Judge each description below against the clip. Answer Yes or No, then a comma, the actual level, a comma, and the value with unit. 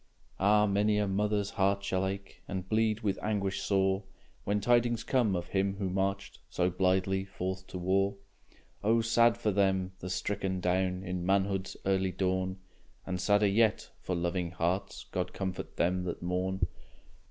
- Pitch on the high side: No, very low, 95 Hz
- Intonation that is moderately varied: No, narrow, 1.7 semitones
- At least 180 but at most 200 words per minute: No, average, 160 wpm